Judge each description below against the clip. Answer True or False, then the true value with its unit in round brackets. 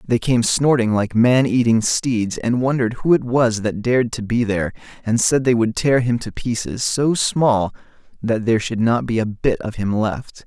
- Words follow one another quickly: True (210 wpm)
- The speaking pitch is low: True (115 Hz)